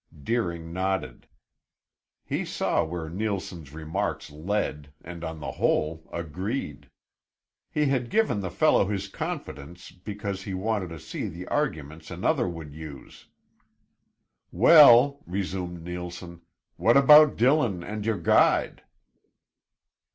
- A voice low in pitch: Yes, very low, 90 Hz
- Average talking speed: No, slow, 115 wpm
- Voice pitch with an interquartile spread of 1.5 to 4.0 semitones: No, average, 5.0 semitones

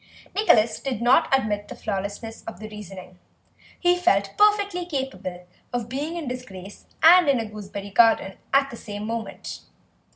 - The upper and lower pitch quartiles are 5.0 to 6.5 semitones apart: Yes, wide, 5.5 semitones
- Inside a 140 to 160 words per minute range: Yes, average, 155 wpm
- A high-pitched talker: Yes, high, 230 Hz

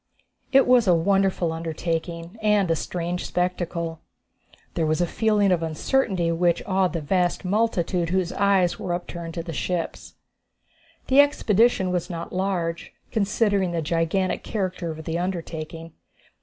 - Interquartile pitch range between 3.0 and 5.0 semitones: No, narrow, 2.6 semitones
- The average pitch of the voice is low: No, medium, 180 Hz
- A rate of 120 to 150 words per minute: Yes, average, 140 wpm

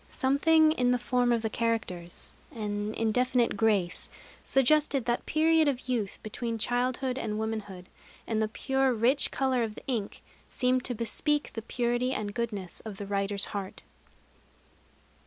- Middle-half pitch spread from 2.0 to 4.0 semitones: Yes, average, 3.3 semitones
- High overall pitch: Yes, high, 235 Hz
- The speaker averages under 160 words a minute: Yes, average, 150 wpm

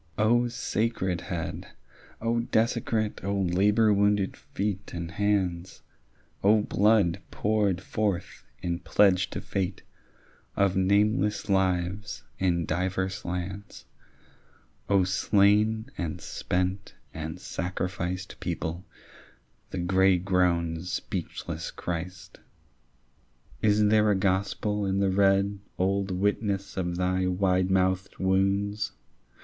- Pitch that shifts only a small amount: Yes, narrow, 2.1 semitones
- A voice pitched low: Yes, very low, 95 Hz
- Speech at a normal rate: No, slow, 105 wpm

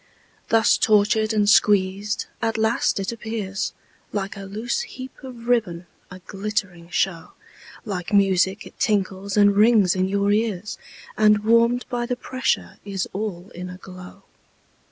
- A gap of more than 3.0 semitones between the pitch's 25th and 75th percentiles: No, narrow, 2.6 semitones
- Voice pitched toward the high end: Yes, high, 205 Hz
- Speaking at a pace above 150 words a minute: No, average, 145 wpm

